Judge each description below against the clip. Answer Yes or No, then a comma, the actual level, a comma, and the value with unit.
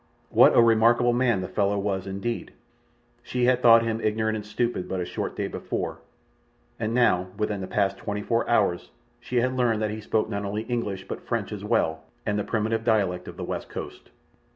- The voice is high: No, low, 110 Hz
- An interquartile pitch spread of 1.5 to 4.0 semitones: Yes, average, 2.9 semitones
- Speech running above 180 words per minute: Yes, average, 200 wpm